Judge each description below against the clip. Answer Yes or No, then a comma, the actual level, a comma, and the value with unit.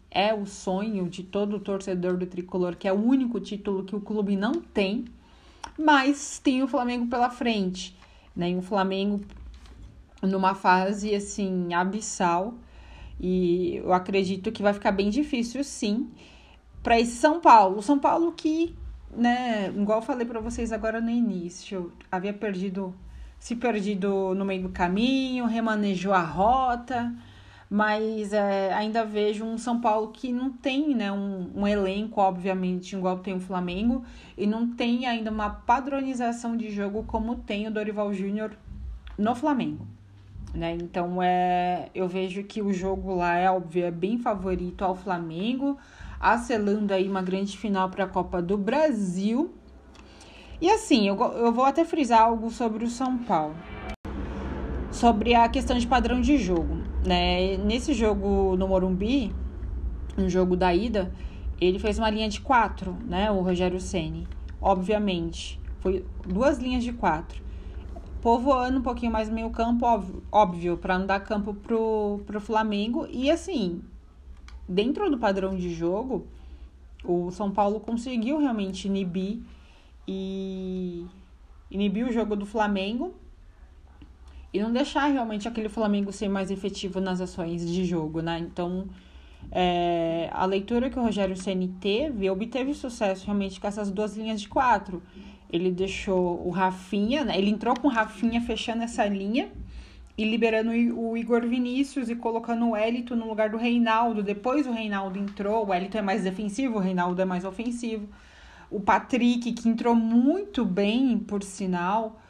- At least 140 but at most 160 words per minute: Yes, average, 155 wpm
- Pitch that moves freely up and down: No, average, 3.9 semitones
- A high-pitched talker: Yes, high, 205 Hz